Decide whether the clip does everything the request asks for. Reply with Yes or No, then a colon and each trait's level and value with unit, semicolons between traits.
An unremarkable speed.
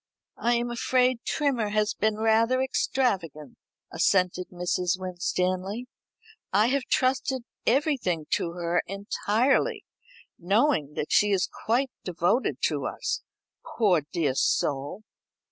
No: slow, 110 wpm